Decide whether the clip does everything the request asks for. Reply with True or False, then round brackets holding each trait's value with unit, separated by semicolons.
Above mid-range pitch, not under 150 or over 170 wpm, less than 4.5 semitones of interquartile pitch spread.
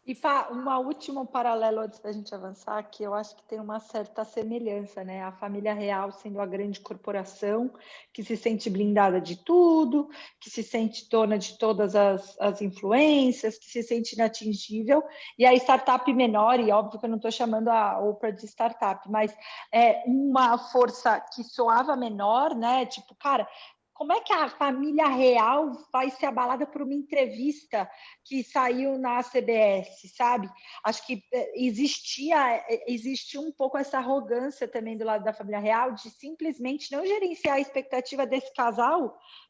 True (240 Hz; 165 wpm; 4.1 semitones)